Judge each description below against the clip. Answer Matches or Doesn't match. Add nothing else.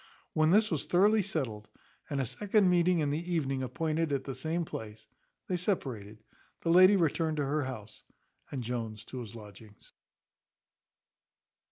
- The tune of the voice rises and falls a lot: Matches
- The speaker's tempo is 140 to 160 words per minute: Matches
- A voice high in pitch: Doesn't match